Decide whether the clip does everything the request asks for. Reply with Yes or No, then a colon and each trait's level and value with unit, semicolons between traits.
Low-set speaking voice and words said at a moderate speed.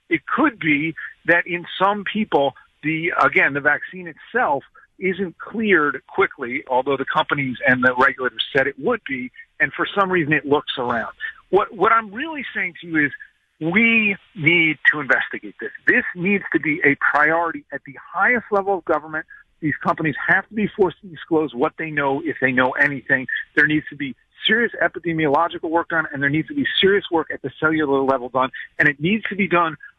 No: medium, 165 Hz; average, 195 wpm